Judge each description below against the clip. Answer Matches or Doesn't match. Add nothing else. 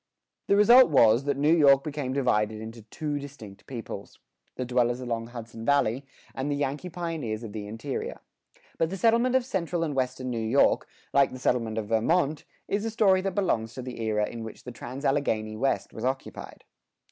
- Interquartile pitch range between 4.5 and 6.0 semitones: Matches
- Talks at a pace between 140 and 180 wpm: Doesn't match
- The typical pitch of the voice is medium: Doesn't match